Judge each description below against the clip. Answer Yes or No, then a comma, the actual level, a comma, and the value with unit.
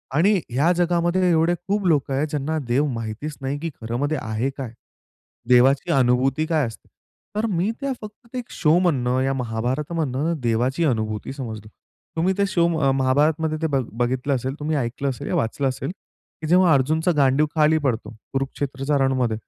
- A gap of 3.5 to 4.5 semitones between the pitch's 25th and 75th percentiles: Yes, average, 4.1 semitones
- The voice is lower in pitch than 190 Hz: Yes, medium, 140 Hz